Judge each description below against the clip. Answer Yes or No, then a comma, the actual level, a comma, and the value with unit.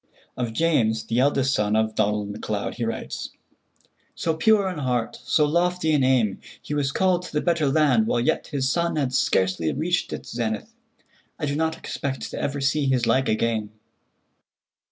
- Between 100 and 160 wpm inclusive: No, average, 175 wpm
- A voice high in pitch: No, low, 135 Hz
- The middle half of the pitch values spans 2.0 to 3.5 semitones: No, wide, 5.6 semitones